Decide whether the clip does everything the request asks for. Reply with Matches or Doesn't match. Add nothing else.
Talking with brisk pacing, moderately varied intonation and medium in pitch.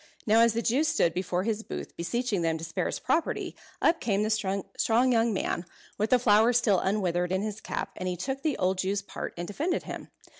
Doesn't match